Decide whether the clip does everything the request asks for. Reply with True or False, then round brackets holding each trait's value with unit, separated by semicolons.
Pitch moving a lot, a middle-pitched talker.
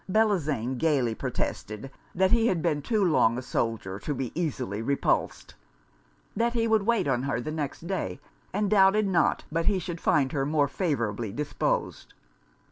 True (7.0 semitones; 155 Hz)